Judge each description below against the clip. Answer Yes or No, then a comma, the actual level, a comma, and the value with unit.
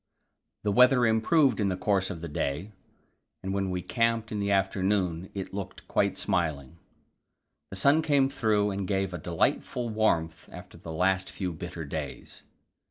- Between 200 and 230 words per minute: No, average, 165 wpm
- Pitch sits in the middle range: No, very low, 95 Hz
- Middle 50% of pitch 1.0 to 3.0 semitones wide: No, average, 3.6 semitones